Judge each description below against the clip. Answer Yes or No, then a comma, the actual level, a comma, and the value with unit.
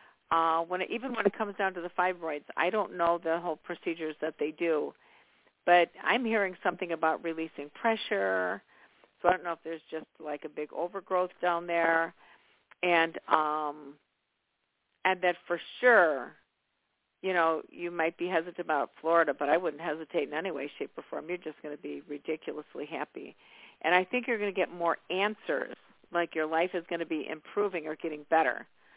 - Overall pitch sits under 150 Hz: No, medium, 170 Hz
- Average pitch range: No, narrow, 2.3 semitones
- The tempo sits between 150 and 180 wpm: No, average, 190 wpm